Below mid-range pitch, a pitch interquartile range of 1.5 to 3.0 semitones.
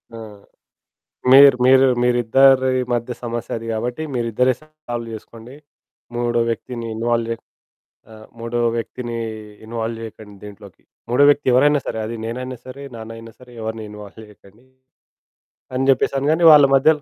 Yes: low, 120 Hz; narrow, 2.6 semitones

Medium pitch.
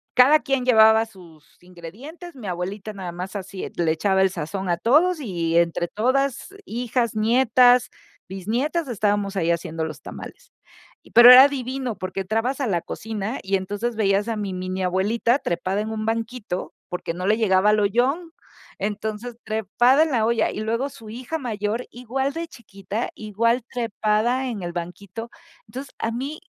No: high, 220 Hz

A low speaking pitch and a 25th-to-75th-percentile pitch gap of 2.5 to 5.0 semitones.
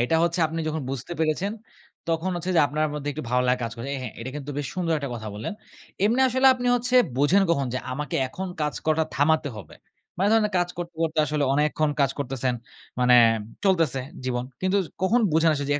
No: medium, 155 Hz; average, 4.6 semitones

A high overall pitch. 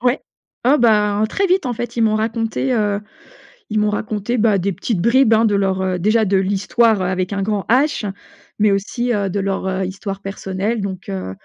Yes: high, 210 Hz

